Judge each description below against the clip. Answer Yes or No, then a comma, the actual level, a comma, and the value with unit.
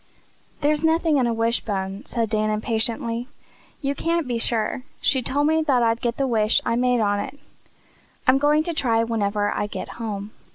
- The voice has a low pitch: No, high, 235 Hz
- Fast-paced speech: No, average, 175 wpm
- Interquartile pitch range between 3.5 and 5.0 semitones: Yes, average, 4.4 semitones